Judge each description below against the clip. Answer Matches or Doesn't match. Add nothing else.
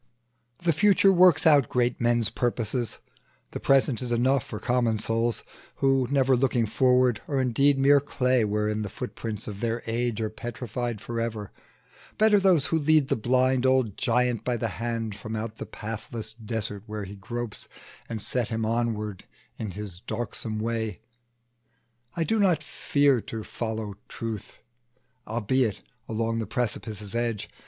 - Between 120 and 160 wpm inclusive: Matches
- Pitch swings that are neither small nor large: Matches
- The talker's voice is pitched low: Matches